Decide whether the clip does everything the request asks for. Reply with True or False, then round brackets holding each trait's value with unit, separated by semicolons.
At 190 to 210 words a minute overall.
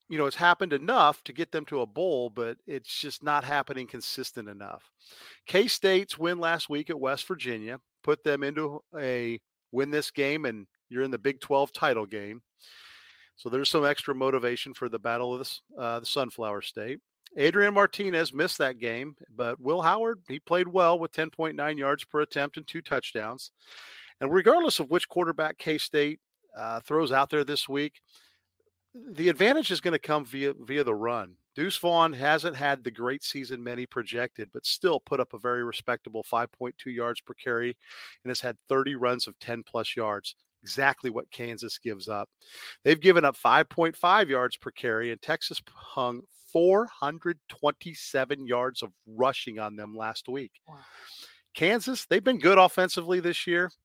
False (175 wpm)